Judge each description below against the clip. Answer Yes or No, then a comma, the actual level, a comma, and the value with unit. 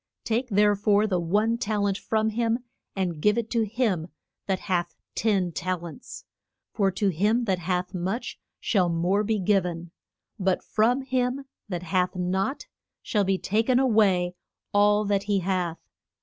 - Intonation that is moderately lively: Yes, average, 3.3 semitones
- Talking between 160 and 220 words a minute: Yes, average, 170 wpm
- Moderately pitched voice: No, high, 200 Hz